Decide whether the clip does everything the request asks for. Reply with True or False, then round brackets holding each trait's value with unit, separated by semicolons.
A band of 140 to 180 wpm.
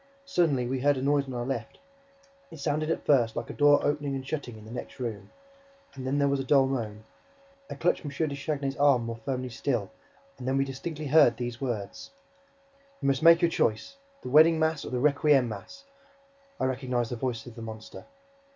False (205 wpm)